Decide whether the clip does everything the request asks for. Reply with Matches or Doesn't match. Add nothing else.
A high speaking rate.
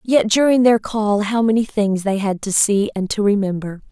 Matches